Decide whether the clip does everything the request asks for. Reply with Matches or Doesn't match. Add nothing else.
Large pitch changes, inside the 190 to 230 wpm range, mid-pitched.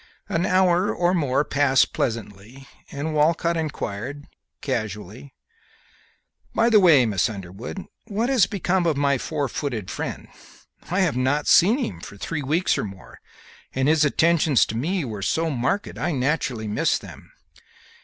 Doesn't match